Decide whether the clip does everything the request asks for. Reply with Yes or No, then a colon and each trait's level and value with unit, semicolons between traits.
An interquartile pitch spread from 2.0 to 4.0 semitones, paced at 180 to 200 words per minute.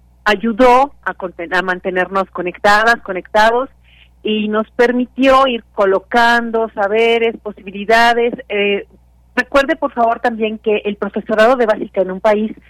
No: average, 3.0 semitones; average, 130 wpm